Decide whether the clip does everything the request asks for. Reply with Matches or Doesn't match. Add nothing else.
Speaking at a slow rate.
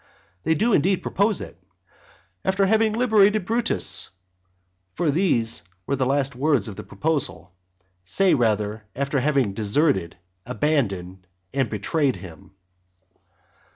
Matches